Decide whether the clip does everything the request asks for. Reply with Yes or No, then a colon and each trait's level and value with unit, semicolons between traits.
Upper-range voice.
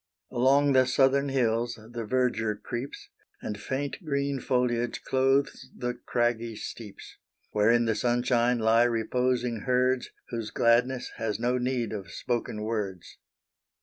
No: low, 120 Hz